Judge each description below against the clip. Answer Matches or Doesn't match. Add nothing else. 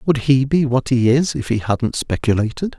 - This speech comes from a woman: Doesn't match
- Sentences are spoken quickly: Matches